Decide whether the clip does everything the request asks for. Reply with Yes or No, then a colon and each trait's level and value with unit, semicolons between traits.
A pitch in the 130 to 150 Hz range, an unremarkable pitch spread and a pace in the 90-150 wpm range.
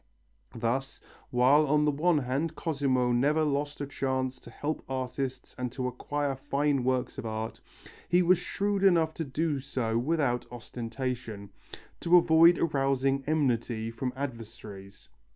Yes: low, 135 Hz; average, 3.6 semitones; average, 140 wpm